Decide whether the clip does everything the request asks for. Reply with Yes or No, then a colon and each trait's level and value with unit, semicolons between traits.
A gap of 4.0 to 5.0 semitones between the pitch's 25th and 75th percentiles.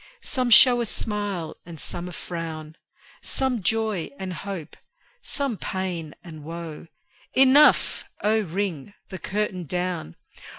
Yes: average, 4.6 semitones